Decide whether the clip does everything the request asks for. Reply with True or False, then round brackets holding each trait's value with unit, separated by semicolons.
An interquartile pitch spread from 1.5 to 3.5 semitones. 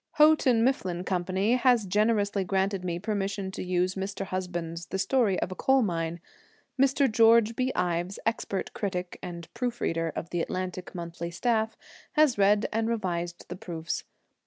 False (4.3 semitones)